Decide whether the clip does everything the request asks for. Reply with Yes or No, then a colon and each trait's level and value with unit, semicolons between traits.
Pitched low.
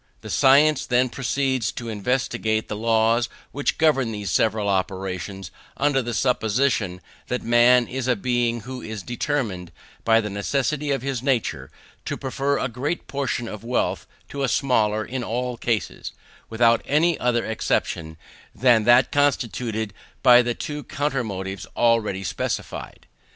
Yes: low, 120 Hz